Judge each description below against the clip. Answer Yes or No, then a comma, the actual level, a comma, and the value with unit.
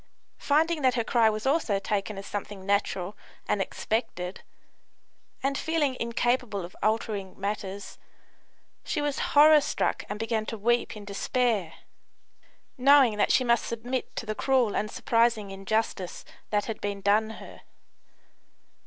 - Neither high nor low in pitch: No, high, 220 Hz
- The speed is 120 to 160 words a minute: Yes, average, 140 wpm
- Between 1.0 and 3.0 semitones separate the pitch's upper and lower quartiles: No, average, 3.7 semitones